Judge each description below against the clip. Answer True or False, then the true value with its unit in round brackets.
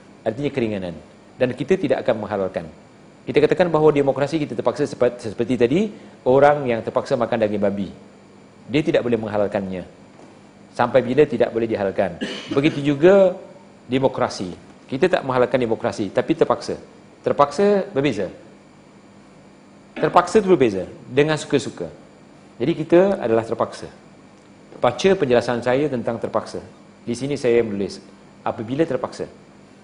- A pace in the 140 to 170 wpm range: False (125 wpm)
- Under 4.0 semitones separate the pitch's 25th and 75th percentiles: False (5.2 semitones)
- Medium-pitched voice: False (125 Hz)